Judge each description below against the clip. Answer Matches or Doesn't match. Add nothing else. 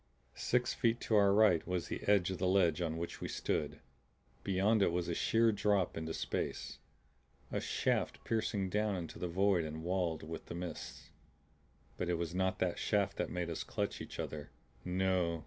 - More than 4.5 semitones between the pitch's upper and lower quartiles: Doesn't match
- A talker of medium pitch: Doesn't match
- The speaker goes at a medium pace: Matches